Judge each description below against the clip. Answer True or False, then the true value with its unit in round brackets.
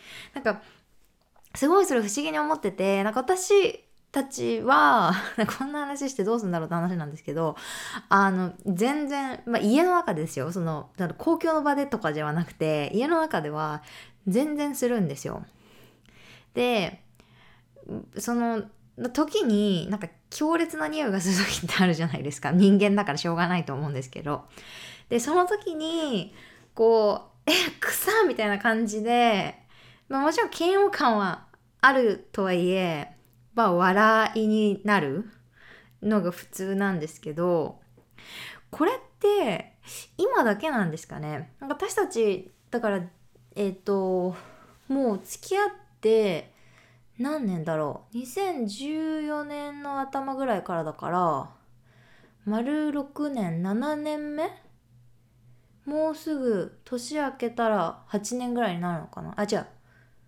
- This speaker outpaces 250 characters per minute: True (260 characters per minute)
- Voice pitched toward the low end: False (210 Hz)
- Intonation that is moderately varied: False (8.6 semitones)